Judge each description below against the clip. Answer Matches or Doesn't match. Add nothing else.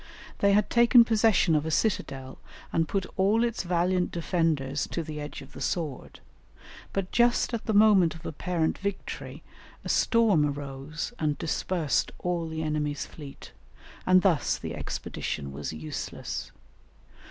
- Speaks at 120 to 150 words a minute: Matches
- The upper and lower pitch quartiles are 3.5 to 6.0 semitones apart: Matches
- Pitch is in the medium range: Matches